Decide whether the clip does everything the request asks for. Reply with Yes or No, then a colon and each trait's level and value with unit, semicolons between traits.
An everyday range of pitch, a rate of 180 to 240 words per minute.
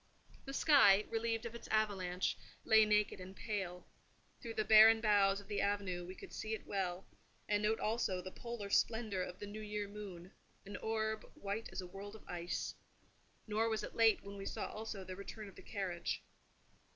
No: narrow, 2.2 semitones; average, 190 wpm